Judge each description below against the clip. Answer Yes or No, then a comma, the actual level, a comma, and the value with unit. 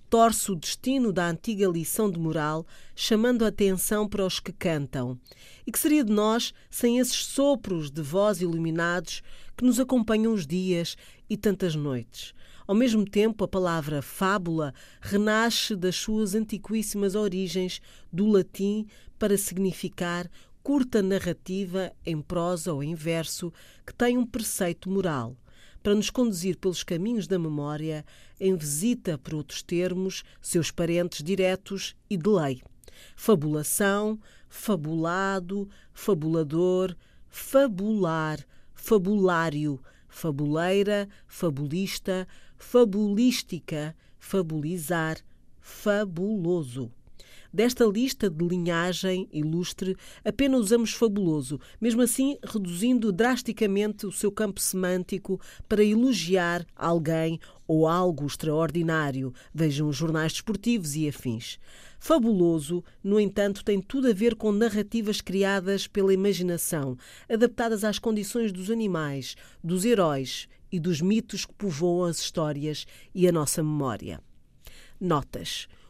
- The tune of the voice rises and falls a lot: No, average, 4.5 semitones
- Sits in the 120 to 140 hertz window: No, medium, 185 Hz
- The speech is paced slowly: Yes, slow, 115 wpm